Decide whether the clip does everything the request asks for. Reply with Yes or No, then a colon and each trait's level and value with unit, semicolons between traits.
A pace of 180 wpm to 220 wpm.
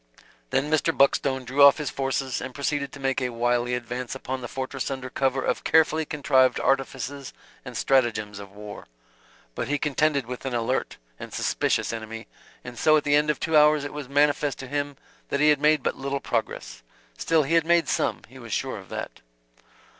Yes: average, 200 wpm